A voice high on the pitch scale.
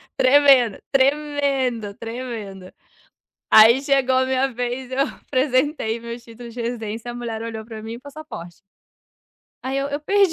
Yes: very high, 250 Hz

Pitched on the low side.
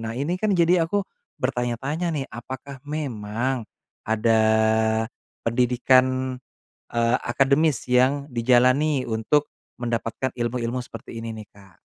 Yes: low, 125 Hz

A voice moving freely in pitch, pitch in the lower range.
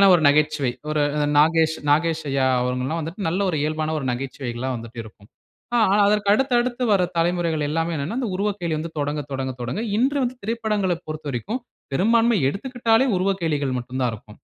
No: wide, 6.9 semitones; medium, 160 Hz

